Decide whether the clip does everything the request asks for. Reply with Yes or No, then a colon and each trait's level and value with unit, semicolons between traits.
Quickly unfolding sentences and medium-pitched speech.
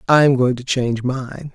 No: fast, 235 wpm; low, 130 Hz